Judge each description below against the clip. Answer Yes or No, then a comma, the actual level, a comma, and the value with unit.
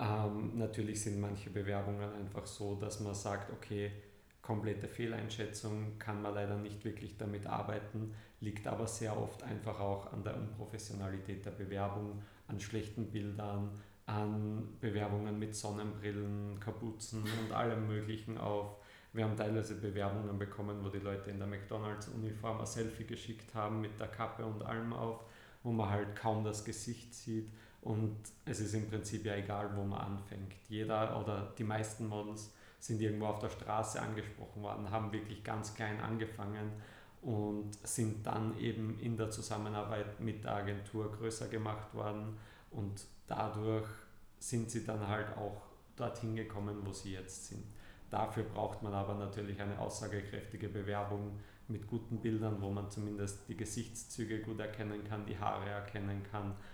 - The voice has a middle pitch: No, low, 105 Hz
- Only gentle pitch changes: Yes, narrow, 1.3 semitones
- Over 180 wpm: No, average, 155 wpm